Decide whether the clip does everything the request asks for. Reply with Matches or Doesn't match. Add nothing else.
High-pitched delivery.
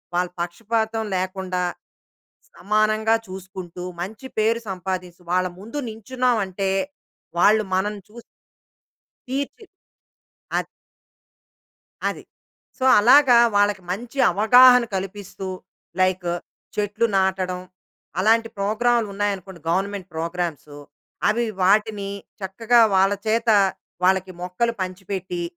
Matches